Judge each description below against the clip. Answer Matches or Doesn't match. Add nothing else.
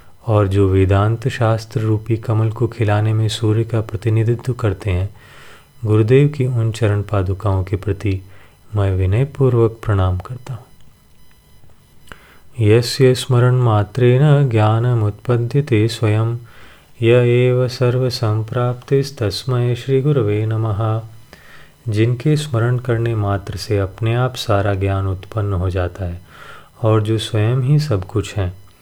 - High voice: Doesn't match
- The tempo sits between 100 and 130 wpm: Matches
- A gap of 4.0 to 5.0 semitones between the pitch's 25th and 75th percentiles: Doesn't match